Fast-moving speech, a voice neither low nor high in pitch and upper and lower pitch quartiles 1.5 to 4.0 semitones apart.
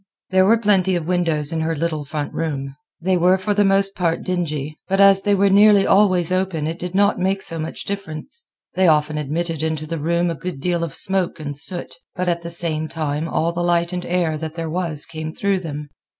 Yes: fast, 220 wpm; medium, 170 Hz; average, 3.1 semitones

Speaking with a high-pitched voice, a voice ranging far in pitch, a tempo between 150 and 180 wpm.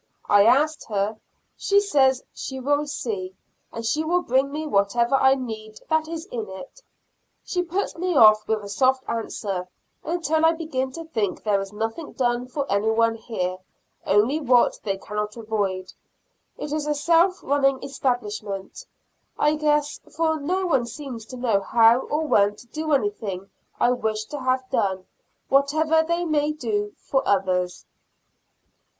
Yes: very high, 255 Hz; wide, 6.2 semitones; average, 160 wpm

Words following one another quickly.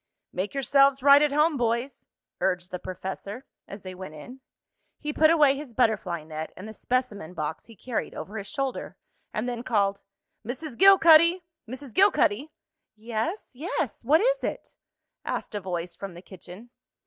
No: average, 160 wpm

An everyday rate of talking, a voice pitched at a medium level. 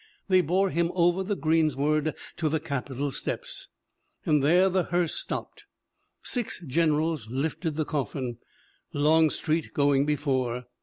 No: slow, 125 wpm; medium, 155 Hz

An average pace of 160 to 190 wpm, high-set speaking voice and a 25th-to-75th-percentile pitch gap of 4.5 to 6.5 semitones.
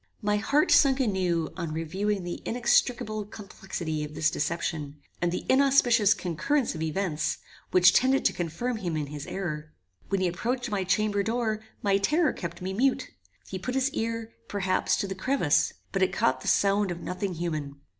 Yes: average, 175 wpm; high, 195 Hz; average, 5.2 semitones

